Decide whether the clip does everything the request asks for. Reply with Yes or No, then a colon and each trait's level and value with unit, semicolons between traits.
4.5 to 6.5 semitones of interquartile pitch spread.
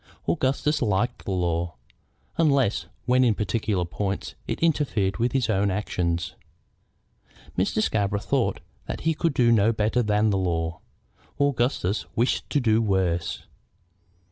Yes: average, 4.8 semitones